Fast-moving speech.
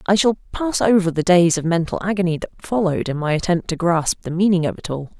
Yes: fast, 245 wpm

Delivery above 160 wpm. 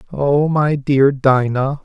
No: slow, 130 wpm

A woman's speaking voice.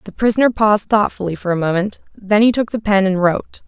Yes: female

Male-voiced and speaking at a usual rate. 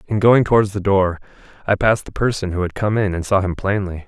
No: male; fast, 250 wpm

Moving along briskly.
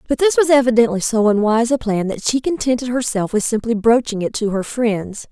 Yes: fast, 215 wpm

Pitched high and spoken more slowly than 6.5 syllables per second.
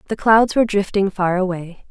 Yes: high, 195 Hz; 5.3 syllables/s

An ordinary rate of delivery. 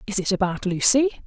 Yes: average, 190 wpm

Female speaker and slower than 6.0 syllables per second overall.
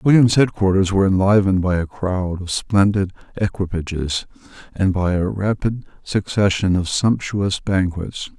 No: male; 4.6 syllables/s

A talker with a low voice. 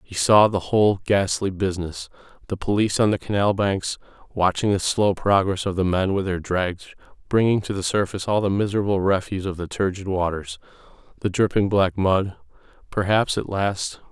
Yes: very low, 95 Hz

